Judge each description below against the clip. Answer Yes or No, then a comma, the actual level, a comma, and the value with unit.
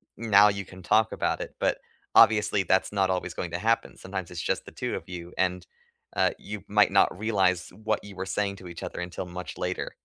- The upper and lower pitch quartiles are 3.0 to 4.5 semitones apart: No, narrow, 2.4 semitones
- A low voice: Yes, very low, 95 Hz